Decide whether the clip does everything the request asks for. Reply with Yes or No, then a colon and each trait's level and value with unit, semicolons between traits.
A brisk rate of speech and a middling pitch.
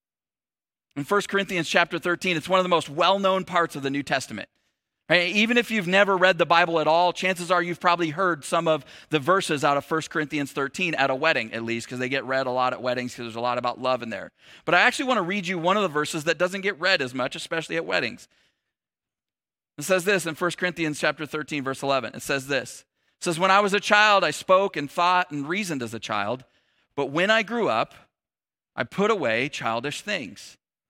Yes: fast, 235 wpm; medium, 165 Hz